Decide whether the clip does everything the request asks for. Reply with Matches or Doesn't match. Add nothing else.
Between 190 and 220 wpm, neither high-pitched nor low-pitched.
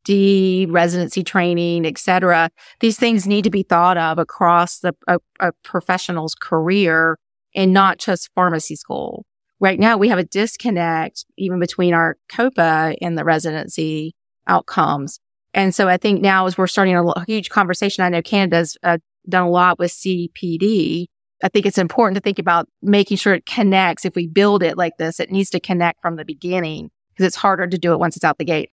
Matches